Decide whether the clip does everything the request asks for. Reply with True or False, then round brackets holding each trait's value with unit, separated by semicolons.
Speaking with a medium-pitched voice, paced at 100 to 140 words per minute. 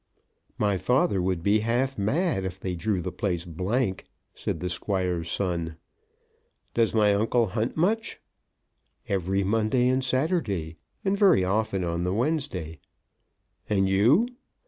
False (100 Hz; 135 wpm)